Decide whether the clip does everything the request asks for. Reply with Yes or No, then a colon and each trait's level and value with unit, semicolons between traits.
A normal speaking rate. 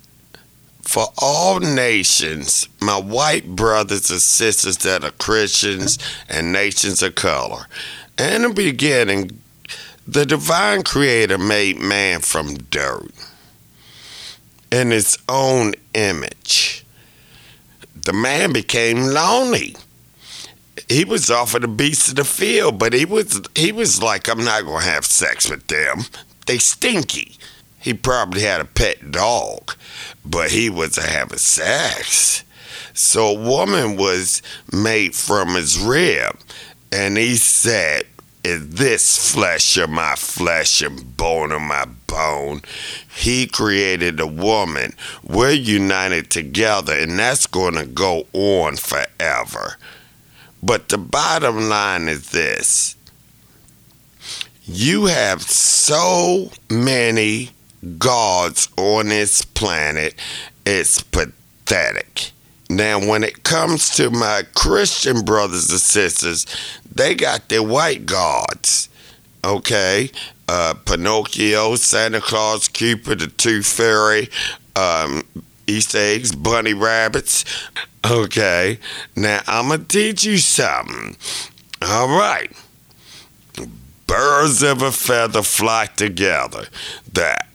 No: slow, 115 wpm